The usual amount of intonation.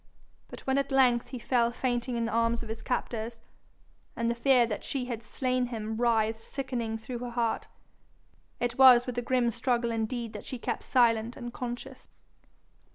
No: narrow, 1.5 semitones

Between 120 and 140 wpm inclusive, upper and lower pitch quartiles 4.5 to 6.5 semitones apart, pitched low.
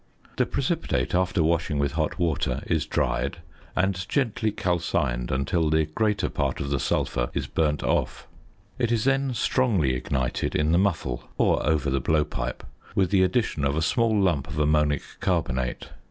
No: average, 165 wpm; wide, 5.4 semitones; very low, 80 Hz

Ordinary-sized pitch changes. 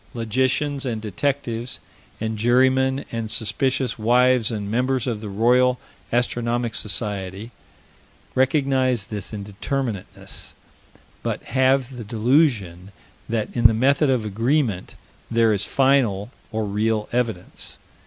Yes: average, 3.4 semitones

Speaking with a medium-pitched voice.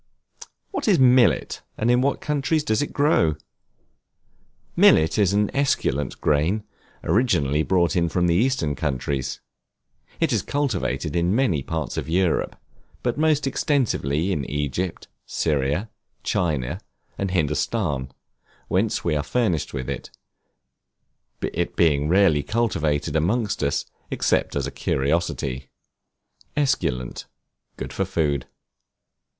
No: very low, 85 Hz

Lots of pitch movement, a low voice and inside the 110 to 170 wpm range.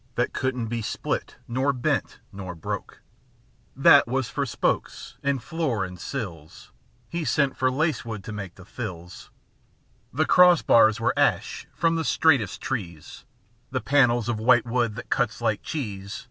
No: average, 4.7 semitones; low, 120 Hz; average, 160 wpm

